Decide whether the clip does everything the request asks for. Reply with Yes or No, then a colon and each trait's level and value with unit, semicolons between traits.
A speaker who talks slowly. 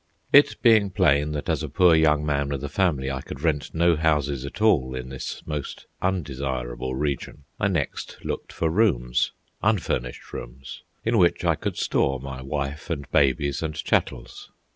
No: average, 170 wpm